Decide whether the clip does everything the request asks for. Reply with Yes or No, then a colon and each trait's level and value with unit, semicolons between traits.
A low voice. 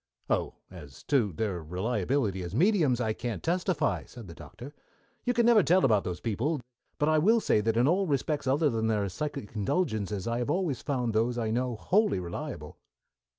Yes: low, 120 Hz